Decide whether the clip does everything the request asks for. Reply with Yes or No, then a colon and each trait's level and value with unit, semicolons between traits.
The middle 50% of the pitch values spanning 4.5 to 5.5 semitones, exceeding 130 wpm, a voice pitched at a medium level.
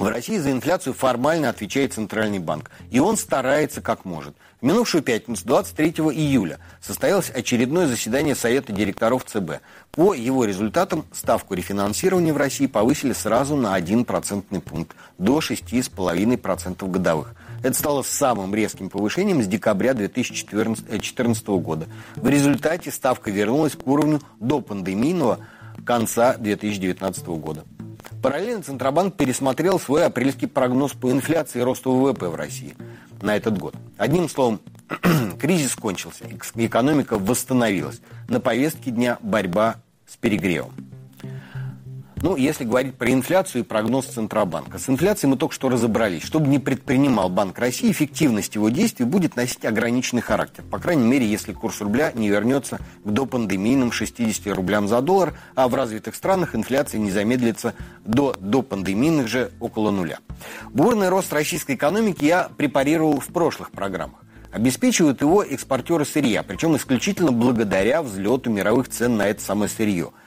No: average, 4.9 semitones; average, 140 wpm; low, 120 Hz